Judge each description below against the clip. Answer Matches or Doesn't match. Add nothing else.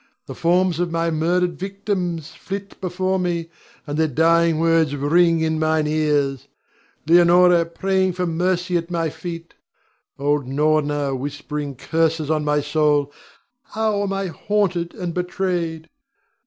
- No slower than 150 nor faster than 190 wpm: Doesn't match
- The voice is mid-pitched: Matches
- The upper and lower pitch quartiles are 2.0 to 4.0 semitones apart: Matches